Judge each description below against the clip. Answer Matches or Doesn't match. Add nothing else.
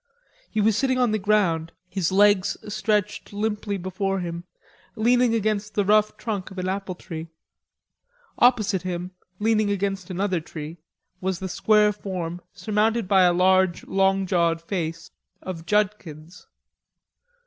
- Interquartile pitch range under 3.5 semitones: Matches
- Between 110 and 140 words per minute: Matches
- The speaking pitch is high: Matches